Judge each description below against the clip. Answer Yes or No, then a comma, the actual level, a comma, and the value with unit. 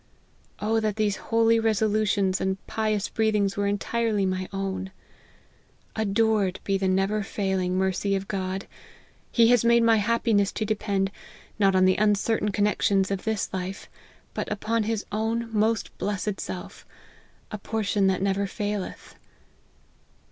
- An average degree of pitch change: No, narrow, 2.2 semitones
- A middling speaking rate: Yes, average, 145 wpm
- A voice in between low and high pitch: No, high, 205 Hz